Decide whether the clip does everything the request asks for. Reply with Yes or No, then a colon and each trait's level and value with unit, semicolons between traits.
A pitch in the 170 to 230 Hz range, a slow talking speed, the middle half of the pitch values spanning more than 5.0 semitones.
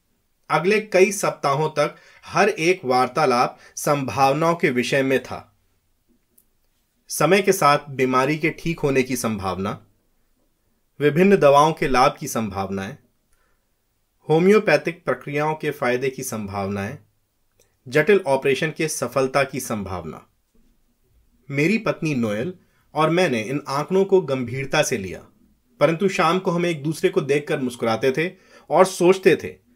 No: medium, 140 Hz; slow, 125 wpm; wide, 5.5 semitones